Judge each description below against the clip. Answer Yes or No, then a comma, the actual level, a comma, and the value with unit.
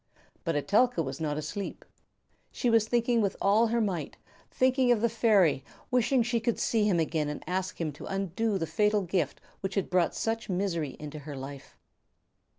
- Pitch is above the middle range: Yes, high, 195 Hz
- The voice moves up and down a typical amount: No, wide, 6.0 semitones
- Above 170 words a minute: Yes, average, 180 wpm